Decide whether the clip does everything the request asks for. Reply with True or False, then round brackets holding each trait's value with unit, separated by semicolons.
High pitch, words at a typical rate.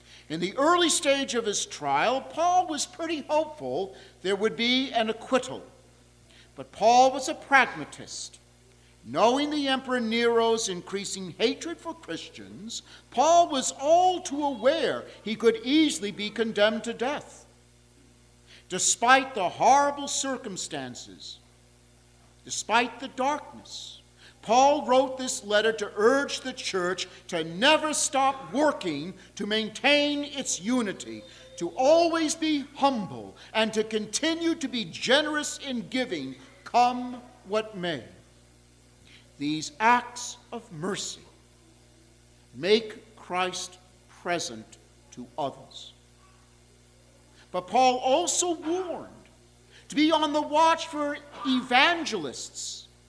False (225 Hz; 110 wpm)